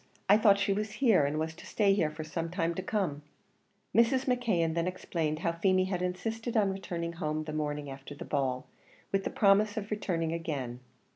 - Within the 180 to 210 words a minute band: Yes, average, 200 wpm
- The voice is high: No, medium, 175 Hz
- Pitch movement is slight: No, average, 4.7 semitones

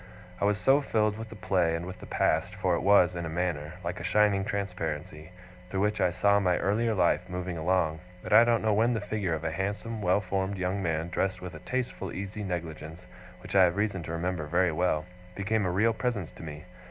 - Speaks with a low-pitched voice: Yes, very low, 95 Hz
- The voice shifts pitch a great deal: No, average, 3.3 semitones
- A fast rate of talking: Yes, fast, 225 wpm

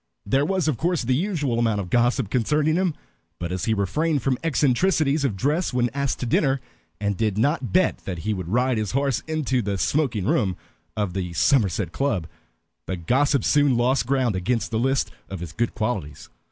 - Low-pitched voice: Yes, low, 125 Hz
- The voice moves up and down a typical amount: No, wide, 5.7 semitones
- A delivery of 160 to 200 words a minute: Yes, average, 195 wpm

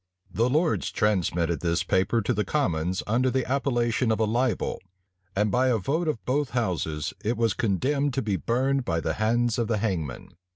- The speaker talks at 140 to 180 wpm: No, average, 190 wpm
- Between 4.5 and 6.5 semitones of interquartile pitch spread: Yes, average, 5.2 semitones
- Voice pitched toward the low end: Yes, low, 115 Hz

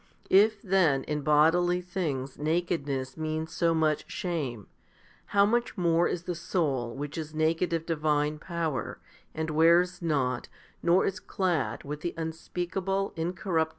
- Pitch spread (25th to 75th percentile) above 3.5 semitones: No, average, 2.9 semitones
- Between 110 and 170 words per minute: Yes, average, 150 wpm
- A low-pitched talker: No, medium, 165 Hz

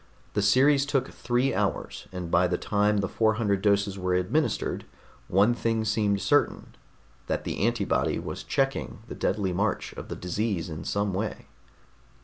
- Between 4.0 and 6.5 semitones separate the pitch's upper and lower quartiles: No, average, 3.4 semitones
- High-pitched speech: No, low, 105 Hz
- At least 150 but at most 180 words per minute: Yes, average, 160 wpm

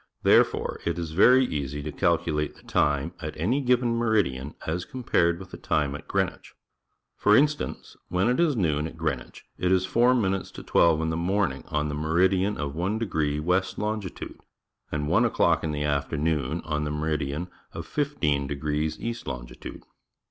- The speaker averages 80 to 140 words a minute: No, average, 170 wpm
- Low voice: Yes, very low, 80 Hz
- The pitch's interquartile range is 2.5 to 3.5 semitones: No, average, 5.3 semitones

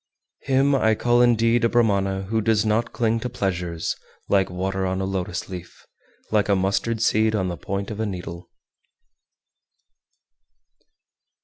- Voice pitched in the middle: No, low, 100 Hz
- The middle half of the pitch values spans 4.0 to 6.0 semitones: No, average, 3.2 semitones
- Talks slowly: No, average, 150 wpm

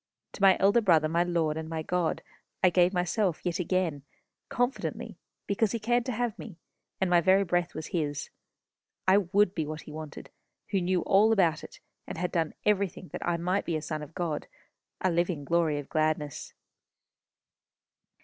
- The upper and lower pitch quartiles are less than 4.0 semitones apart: Yes, average, 3.4 semitones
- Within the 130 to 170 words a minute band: No, average, 180 wpm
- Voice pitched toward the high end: No, medium, 175 Hz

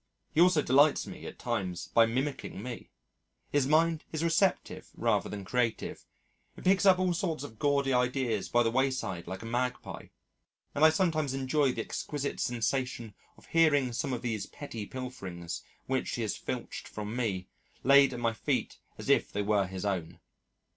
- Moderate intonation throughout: Yes, average, 4.7 semitones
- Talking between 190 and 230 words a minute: No, average, 175 wpm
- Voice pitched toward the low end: Yes, low, 125 Hz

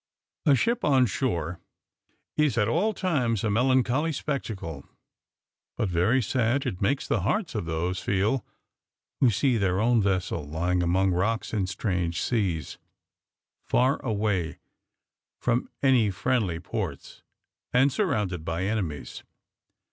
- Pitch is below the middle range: Yes, low, 110 Hz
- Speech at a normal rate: No, slow, 125 wpm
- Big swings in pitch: Yes, wide, 6.3 semitones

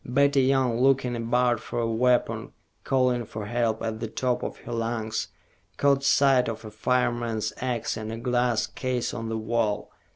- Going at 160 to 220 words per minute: Yes, average, 170 wpm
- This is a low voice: Yes, low, 120 Hz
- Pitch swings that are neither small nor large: No, narrow, 2.0 semitones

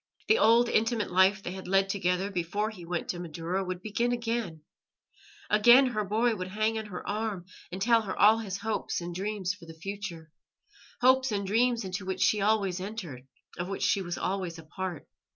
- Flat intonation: No, average, 3.3 semitones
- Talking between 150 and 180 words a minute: No, average, 190 wpm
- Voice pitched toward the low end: No, high, 195 Hz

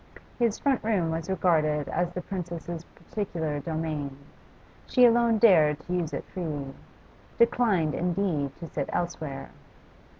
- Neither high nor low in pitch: Yes, medium, 170 Hz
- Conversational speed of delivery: No, slow, 130 wpm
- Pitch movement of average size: Yes, average, 4.4 semitones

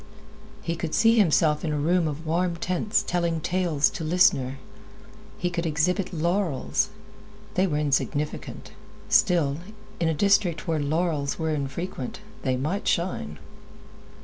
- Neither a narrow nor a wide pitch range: Yes, average, 3.2 semitones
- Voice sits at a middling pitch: Yes, medium, 165 Hz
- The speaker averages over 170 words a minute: No, slow, 135 wpm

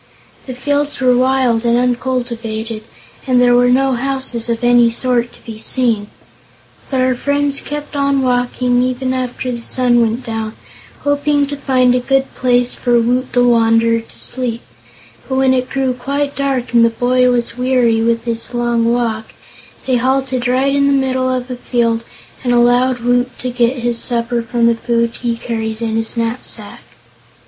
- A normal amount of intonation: No, narrow, 1.8 semitones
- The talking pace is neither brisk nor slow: Yes, average, 175 wpm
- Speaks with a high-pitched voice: Yes, high, 245 Hz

